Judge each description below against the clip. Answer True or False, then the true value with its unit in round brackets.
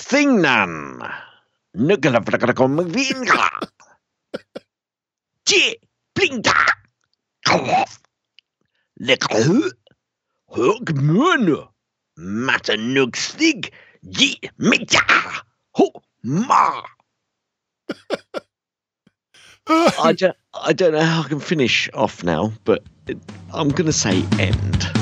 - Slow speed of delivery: True (80 wpm)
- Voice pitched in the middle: True (160 Hz)